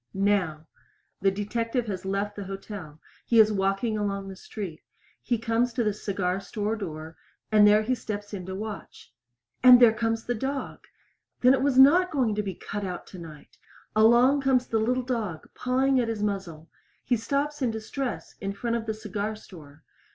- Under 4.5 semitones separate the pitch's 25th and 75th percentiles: Yes, average, 3.6 semitones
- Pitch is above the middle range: Yes, high, 215 Hz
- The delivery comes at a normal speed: Yes, average, 180 wpm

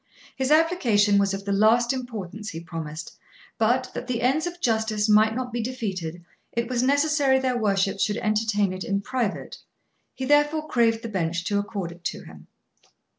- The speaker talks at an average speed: Yes, average, 175 wpm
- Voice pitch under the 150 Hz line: No, high, 220 Hz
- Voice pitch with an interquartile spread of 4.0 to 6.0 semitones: Yes, average, 4.4 semitones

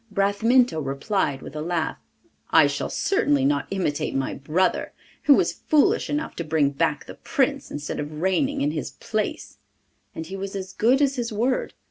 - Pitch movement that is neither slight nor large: No, wide, 8.3 semitones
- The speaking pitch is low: No, high, 190 Hz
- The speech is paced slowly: No, average, 175 wpm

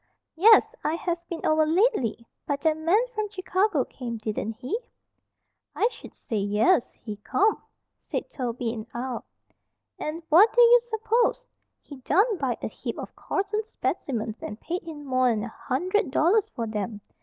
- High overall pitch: Yes, very high, 315 Hz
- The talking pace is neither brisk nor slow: Yes, average, 155 wpm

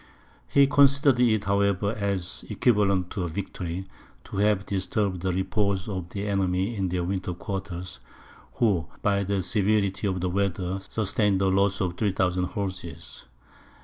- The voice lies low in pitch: Yes, very low, 95 Hz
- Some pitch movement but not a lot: No, narrow, 1.8 semitones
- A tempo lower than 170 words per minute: Yes, average, 145 wpm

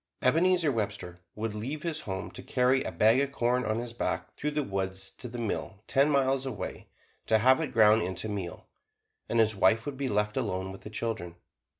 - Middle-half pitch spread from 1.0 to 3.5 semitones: No, average, 4.5 semitones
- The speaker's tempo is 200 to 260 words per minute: Yes, fast, 205 wpm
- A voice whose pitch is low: Yes, low, 115 Hz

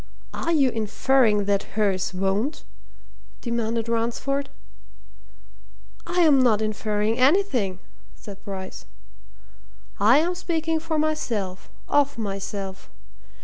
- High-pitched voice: Yes, high, 230 Hz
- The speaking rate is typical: No, slow, 95 wpm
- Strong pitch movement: Yes, wide, 6.0 semitones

